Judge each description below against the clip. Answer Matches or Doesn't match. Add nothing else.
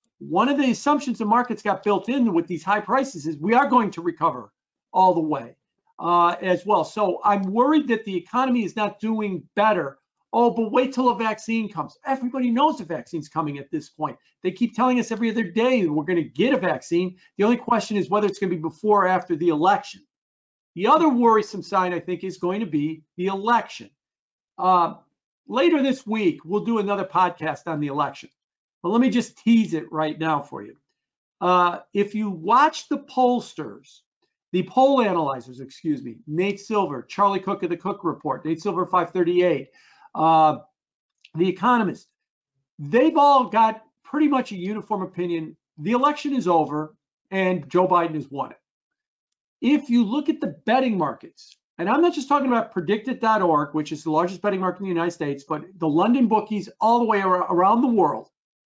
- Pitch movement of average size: Doesn't match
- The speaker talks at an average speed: Matches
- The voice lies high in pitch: Matches